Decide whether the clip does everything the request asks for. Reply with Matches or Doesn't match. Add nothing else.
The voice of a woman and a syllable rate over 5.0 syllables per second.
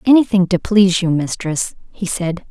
Doesn't match